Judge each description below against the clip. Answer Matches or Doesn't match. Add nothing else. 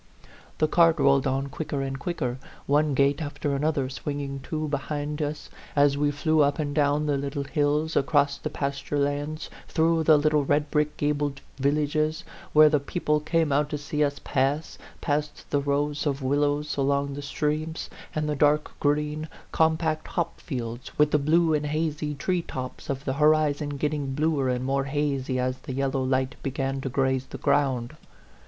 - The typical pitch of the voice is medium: Matches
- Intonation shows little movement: Matches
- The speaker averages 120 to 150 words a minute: Doesn't match